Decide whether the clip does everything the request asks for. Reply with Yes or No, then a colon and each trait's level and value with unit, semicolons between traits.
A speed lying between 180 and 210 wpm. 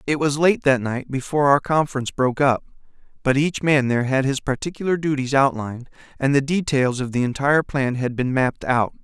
Yes: average, 200 wpm